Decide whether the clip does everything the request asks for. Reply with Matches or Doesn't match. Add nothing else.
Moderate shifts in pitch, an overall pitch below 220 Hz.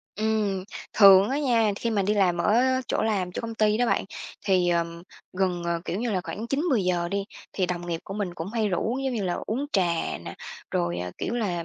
Matches